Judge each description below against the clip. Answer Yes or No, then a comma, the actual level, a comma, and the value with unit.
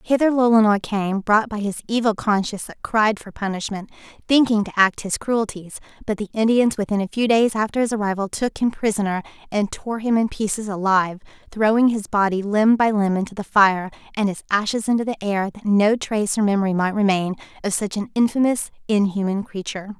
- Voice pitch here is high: Yes, high, 210 Hz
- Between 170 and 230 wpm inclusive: Yes, average, 190 wpm